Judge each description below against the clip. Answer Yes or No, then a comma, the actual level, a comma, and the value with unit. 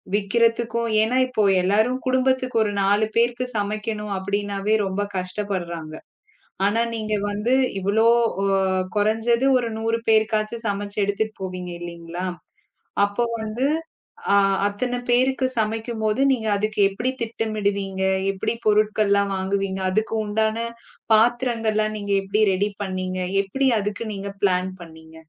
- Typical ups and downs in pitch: No, narrow, 2.3 semitones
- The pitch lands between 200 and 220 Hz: Yes, high, 210 Hz